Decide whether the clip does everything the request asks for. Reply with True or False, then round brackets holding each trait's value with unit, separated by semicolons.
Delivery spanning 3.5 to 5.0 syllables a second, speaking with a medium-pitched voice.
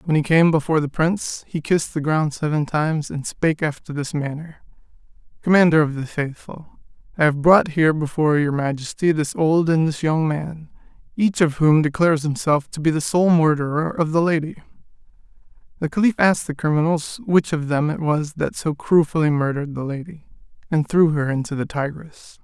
False (5.4 syllables/s; 155 Hz)